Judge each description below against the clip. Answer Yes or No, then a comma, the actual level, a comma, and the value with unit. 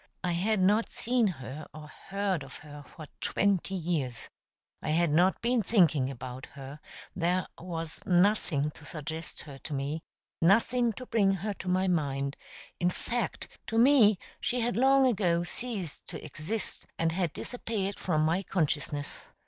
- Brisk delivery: No, average, 155 wpm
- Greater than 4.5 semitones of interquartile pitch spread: Yes, average, 5.3 semitones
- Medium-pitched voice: Yes, medium, 175 Hz